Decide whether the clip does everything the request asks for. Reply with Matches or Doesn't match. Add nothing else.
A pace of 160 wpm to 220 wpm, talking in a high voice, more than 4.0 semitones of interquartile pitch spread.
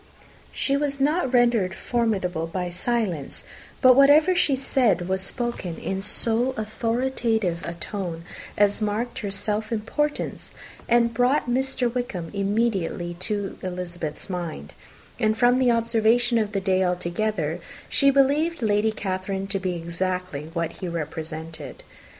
Doesn't match